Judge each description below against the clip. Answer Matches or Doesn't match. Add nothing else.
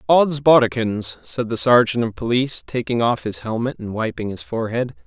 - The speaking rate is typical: Matches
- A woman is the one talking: Doesn't match